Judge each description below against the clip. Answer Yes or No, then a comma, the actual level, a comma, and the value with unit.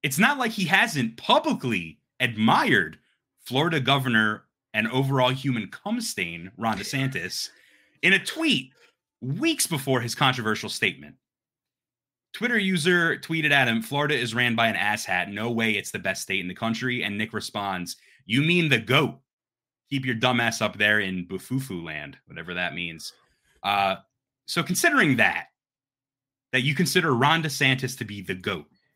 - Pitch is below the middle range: Yes, low, 130 Hz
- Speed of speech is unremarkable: Yes, average, 155 wpm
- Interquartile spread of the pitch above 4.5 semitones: Yes, average, 5.2 semitones